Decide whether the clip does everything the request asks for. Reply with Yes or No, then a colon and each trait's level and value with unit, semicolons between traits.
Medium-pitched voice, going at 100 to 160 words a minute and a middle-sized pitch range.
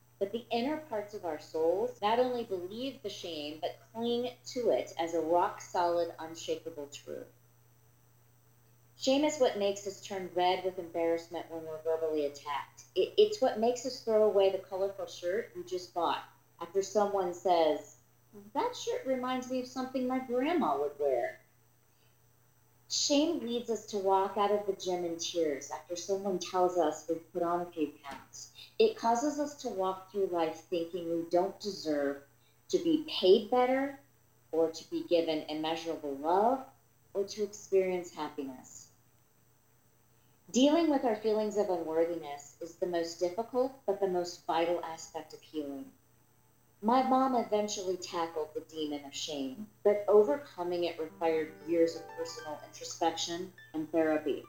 No: medium, 175 Hz; average, 155 wpm; wide, 5.7 semitones